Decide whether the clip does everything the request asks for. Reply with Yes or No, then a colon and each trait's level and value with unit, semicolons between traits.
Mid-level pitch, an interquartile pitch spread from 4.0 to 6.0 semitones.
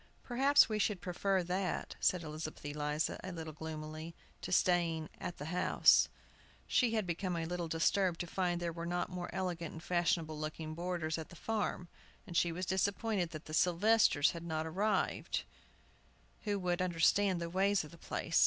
No: medium, 175 Hz; narrow, 2.6 semitones